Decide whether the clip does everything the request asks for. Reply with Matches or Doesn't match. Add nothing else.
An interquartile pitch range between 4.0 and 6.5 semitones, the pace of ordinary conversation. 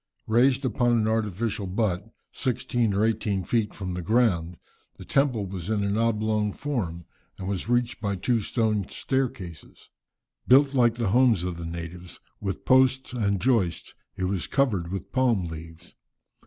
Matches